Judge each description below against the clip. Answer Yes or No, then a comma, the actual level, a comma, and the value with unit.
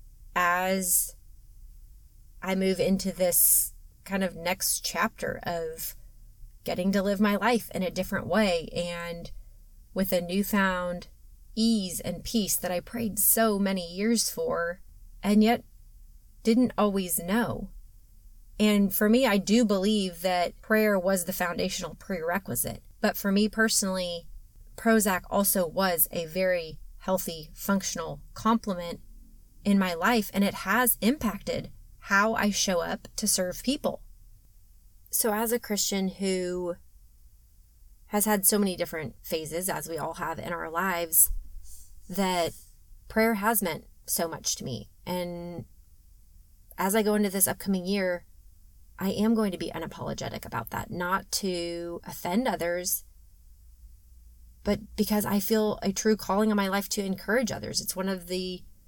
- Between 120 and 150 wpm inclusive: Yes, average, 140 wpm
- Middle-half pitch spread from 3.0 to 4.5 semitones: Yes, average, 3.7 semitones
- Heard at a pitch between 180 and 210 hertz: Yes, medium, 185 Hz